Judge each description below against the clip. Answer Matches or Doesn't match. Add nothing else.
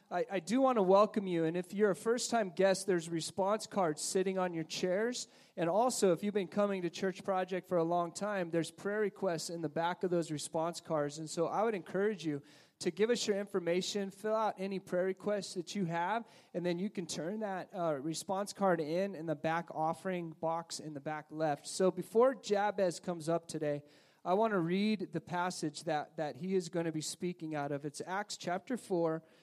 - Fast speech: Matches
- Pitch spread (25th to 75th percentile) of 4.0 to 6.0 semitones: Doesn't match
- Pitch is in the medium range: Matches